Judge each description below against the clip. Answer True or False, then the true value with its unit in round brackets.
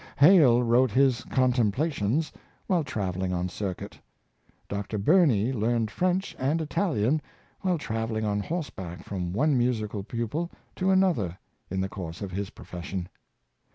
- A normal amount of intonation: False (7.1 semitones)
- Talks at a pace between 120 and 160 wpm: True (140 wpm)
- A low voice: True (115 Hz)